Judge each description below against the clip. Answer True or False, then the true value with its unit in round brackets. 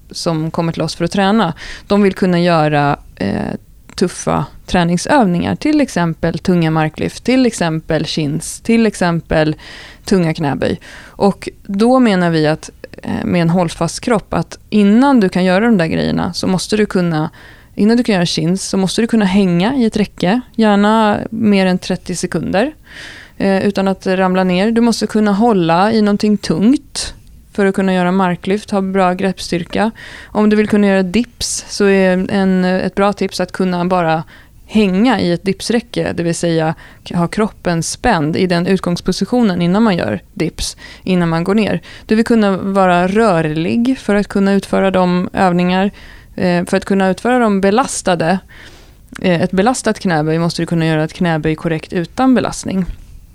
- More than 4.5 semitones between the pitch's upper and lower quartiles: False (3.6 semitones)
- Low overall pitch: False (190 Hz)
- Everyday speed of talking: True (170 wpm)